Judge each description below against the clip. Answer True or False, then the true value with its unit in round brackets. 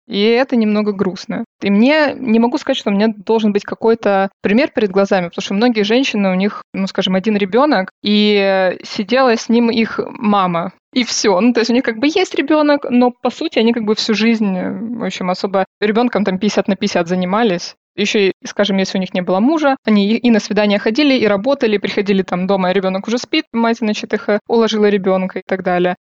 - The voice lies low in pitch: False (215 Hz)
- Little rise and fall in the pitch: False (3.2 semitones)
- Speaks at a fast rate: True (215 wpm)